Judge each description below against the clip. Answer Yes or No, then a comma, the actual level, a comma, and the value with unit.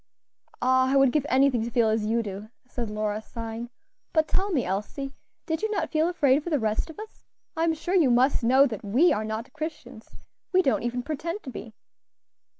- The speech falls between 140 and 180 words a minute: No, fast, 205 wpm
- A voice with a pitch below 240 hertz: No, very high, 260 Hz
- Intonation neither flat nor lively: No, wide, 5.7 semitones